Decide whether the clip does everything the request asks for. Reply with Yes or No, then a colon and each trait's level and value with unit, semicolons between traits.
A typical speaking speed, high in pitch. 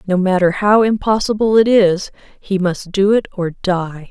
Yes: average, 175 wpm; high, 195 Hz